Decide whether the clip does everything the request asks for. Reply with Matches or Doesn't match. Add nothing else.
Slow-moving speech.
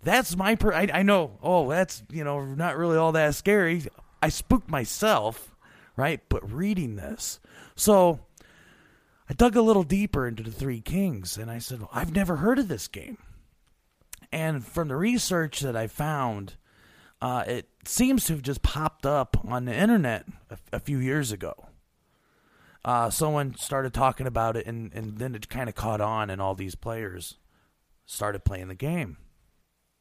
Doesn't match